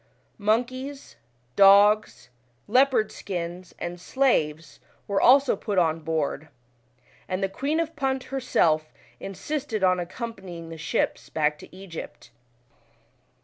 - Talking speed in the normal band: No, slow, 115 wpm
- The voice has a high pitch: Yes, high, 195 Hz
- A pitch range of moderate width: No, wide, 7.3 semitones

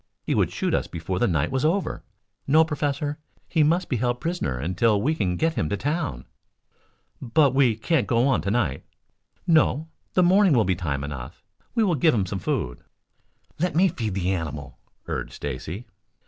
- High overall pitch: No, low, 120 Hz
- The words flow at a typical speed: Yes, average, 185 wpm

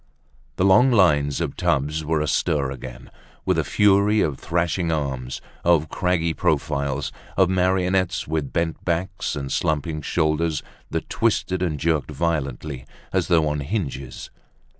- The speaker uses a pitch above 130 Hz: No, very low, 80 Hz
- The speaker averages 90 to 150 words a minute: Yes, average, 140 wpm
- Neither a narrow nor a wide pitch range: Yes, average, 4.1 semitones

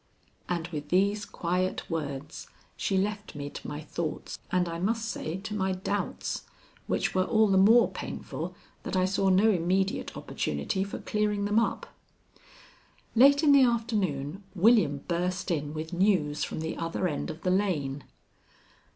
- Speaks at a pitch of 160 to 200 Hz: Yes, medium, 185 Hz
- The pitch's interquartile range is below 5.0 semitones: Yes, average, 4.4 semitones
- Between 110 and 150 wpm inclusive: No, average, 160 wpm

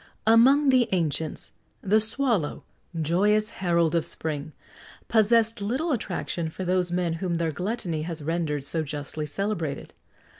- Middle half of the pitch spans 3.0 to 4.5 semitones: No, average, 5.3 semitones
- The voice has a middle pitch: Yes, medium, 175 Hz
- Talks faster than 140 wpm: No, slow, 135 wpm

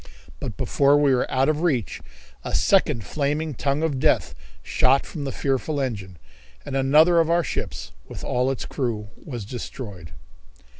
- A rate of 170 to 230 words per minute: No, average, 160 wpm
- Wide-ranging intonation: No, average, 3.6 semitones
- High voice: No, low, 135 Hz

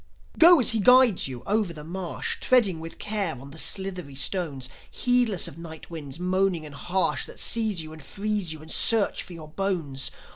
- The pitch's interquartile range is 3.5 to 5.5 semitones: Yes, average, 4.8 semitones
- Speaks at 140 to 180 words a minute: No, average, 190 wpm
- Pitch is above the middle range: No, medium, 180 Hz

